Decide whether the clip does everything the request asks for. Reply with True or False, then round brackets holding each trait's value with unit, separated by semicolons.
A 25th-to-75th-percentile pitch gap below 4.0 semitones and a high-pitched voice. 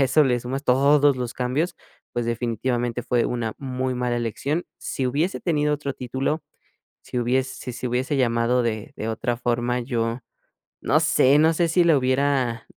False (2.8 semitones; 125 Hz)